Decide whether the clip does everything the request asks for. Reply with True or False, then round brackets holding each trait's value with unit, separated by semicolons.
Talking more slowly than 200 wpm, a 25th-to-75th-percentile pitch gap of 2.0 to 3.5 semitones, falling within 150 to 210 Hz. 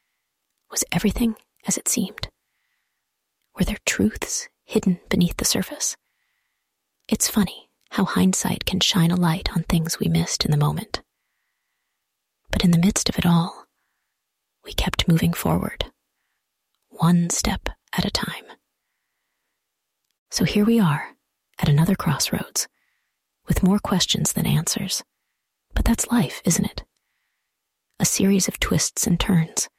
False (135 wpm; 4.0 semitones; 190 Hz)